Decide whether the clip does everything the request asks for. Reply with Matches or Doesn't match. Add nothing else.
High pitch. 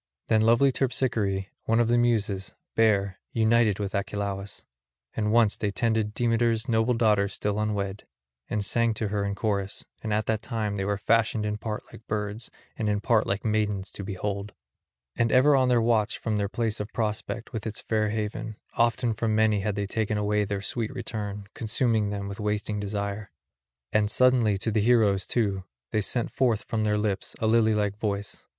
Doesn't match